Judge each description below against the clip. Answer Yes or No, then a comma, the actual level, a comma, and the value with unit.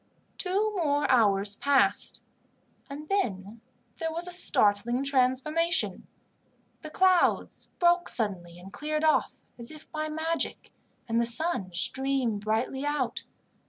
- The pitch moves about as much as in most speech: No, wide, 6.2 semitones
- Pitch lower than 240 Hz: No, very high, 280 Hz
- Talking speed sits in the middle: No, slow, 125 wpm